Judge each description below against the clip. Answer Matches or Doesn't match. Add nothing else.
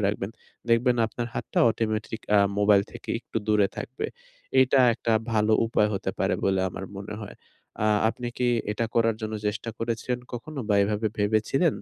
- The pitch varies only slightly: Matches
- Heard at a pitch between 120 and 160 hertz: Doesn't match